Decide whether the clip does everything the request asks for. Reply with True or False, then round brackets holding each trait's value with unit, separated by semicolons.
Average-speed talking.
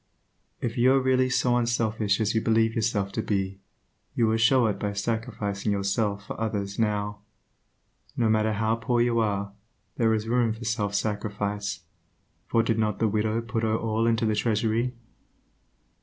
True (170 wpm)